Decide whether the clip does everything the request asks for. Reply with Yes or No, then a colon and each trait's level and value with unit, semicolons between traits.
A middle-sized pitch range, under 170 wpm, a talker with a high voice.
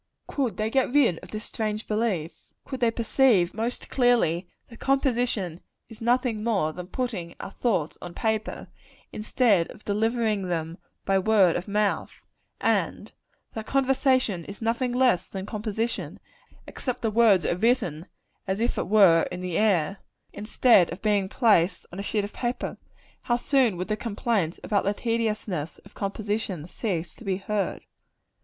Yes: average, 4.1 semitones; average, 160 wpm; high, 215 Hz